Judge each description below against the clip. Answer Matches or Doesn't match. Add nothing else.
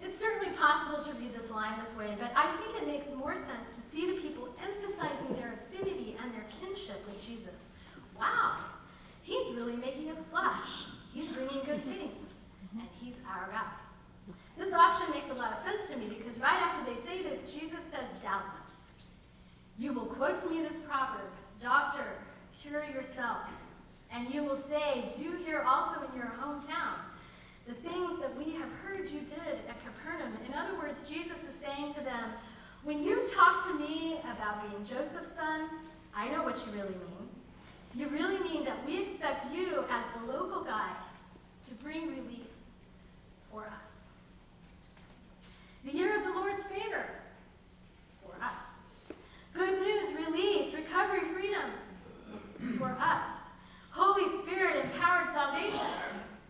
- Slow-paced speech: Doesn't match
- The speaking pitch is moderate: Doesn't match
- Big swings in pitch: Matches